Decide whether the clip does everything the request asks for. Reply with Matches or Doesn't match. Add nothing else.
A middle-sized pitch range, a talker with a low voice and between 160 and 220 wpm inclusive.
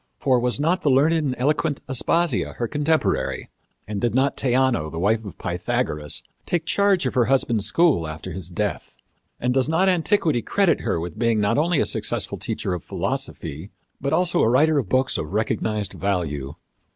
Doesn't match